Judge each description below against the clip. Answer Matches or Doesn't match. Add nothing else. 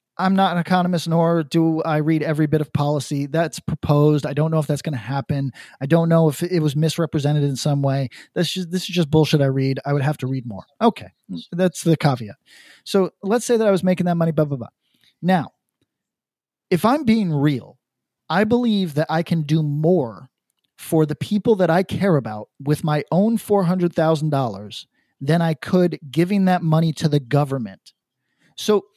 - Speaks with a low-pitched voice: Doesn't match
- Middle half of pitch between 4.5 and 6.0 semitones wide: Doesn't match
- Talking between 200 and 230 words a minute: Matches